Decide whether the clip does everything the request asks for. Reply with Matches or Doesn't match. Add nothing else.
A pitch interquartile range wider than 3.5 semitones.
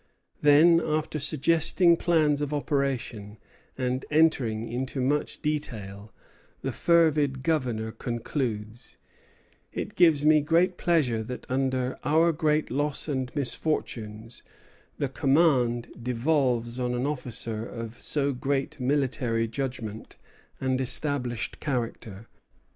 Matches